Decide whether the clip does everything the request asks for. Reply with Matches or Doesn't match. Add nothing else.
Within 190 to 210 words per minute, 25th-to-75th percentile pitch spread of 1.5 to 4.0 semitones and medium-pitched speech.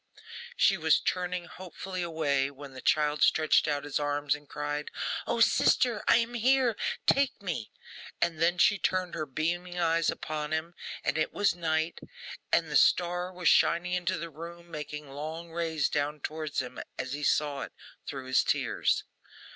Doesn't match